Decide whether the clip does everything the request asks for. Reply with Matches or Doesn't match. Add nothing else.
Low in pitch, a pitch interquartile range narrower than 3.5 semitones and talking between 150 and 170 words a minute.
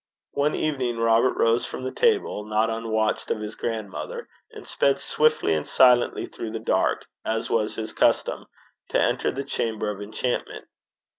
Matches